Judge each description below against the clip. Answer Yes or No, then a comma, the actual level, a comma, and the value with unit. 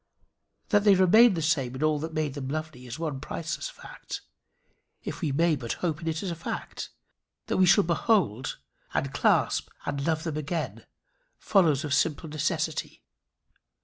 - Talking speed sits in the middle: Yes, average, 175 wpm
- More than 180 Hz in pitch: No, medium, 160 Hz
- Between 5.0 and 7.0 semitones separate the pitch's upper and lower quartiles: No, average, 2.9 semitones